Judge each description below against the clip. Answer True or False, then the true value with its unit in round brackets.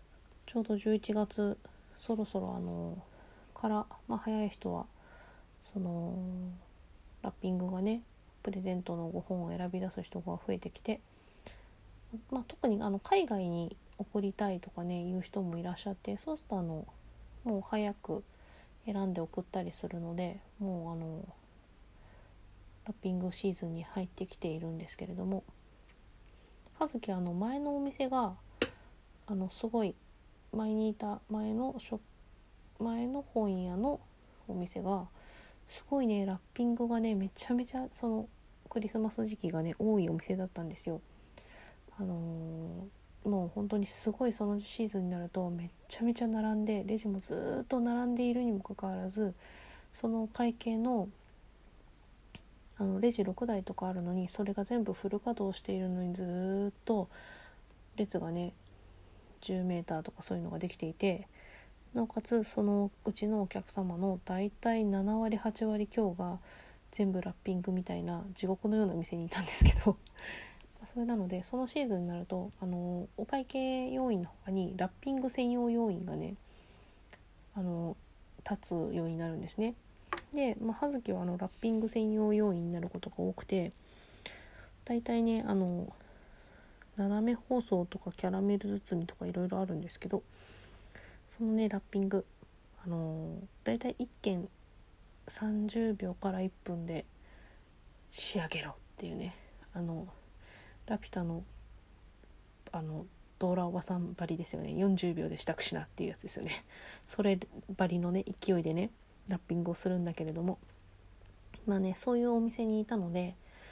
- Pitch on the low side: False (195 Hz)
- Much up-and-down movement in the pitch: False (3.7 semitones)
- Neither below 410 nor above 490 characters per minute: False (285 characters per minute)